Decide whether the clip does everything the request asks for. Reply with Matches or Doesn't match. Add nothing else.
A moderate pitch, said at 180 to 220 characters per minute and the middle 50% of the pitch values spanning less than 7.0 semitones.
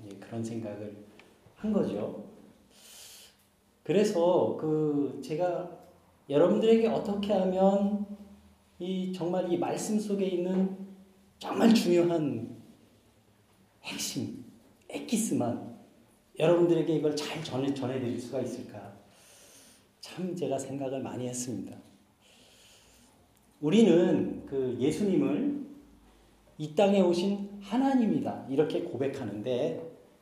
Doesn't match